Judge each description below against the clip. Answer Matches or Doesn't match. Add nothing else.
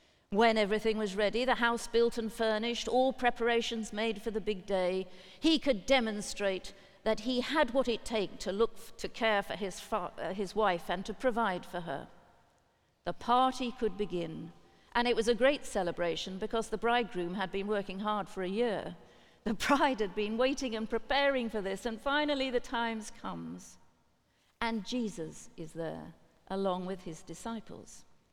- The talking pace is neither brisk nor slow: Matches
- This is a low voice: Doesn't match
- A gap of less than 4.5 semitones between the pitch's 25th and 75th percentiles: Matches